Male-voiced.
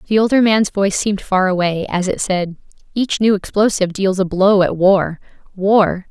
No: female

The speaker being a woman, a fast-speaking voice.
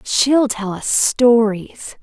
No: female; slow, 120 wpm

